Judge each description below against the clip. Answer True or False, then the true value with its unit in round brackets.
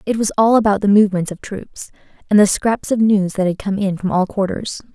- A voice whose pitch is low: False (200 Hz)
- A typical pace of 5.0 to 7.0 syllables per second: True (5.6 syllables/s)